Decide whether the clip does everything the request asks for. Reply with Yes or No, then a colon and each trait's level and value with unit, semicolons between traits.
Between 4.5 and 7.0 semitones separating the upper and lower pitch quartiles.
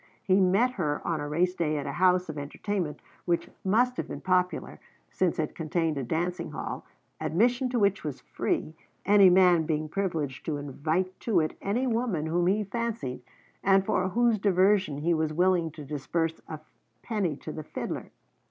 No: average, 4.1 semitones